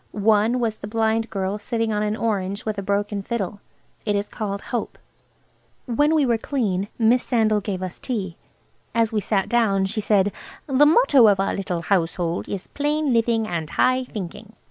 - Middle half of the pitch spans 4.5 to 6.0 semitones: No, average, 2.9 semitones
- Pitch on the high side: Yes, high, 215 Hz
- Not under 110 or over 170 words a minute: No, average, 180 wpm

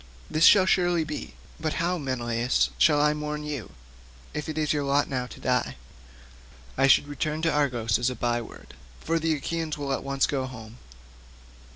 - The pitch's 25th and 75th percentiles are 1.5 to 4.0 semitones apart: Yes, average, 3.6 semitones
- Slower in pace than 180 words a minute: No, average, 185 wpm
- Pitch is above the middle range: No, medium, 145 Hz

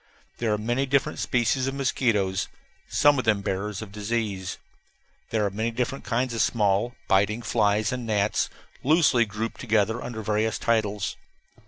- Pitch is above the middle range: No, low, 110 Hz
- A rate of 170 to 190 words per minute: No, average, 155 wpm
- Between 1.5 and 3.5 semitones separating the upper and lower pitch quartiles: Yes, average, 2.7 semitones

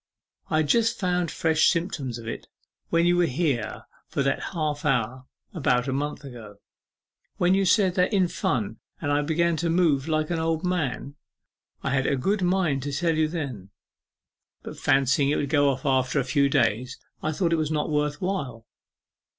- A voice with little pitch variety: No, average, 4.3 semitones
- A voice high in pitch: No, medium, 150 Hz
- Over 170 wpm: Yes, average, 185 wpm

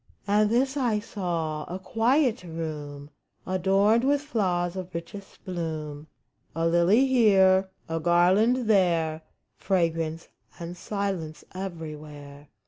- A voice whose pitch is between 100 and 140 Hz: No, medium, 180 Hz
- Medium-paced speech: No, slow, 120 wpm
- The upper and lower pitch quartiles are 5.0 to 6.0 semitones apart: No, average, 4.3 semitones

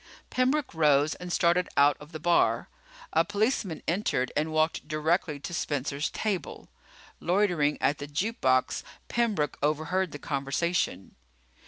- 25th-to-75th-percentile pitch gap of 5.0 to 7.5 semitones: No, average, 3.8 semitones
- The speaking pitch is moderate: Yes, medium, 160 Hz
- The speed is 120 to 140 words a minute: Yes, slow, 135 wpm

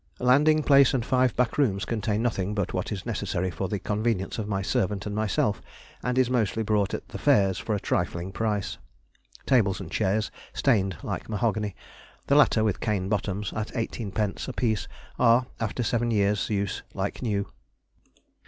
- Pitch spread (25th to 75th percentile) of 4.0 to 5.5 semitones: No, average, 3.0 semitones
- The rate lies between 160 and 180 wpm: Yes, average, 170 wpm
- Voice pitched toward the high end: No, low, 105 Hz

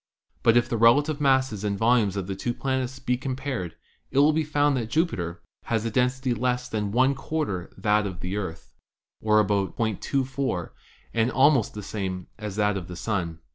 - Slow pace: No, average, 185 wpm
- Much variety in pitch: No, average, 4.9 semitones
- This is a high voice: No, low, 115 Hz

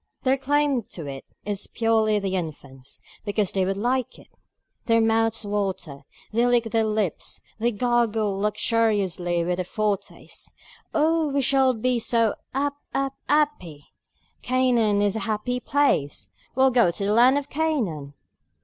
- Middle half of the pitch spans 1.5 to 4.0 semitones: No, average, 4.6 semitones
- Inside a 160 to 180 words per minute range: No, average, 150 wpm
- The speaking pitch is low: No, high, 225 Hz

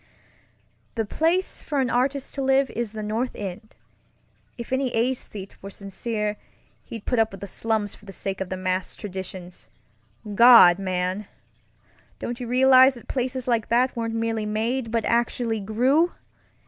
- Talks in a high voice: Yes, high, 225 Hz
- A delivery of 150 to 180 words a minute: Yes, average, 160 wpm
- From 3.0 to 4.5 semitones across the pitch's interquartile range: Yes, average, 3.9 semitones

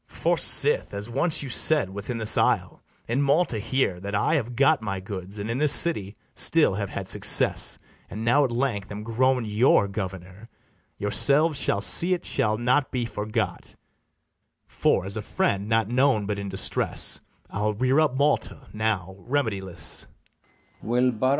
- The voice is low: Yes, low, 110 Hz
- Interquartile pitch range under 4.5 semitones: No, average, 4.8 semitones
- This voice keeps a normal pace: Yes, average, 160 wpm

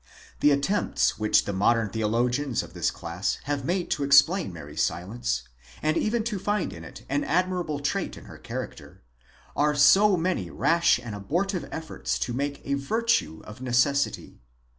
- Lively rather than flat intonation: Yes, wide, 7.2 semitones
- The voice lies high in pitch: No, medium, 145 Hz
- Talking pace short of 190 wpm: Yes, average, 160 wpm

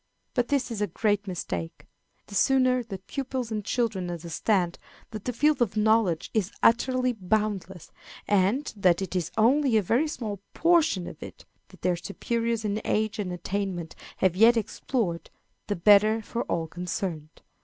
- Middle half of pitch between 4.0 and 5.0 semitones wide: Yes, average, 4.4 semitones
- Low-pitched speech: No, high, 210 Hz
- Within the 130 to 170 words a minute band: Yes, average, 160 wpm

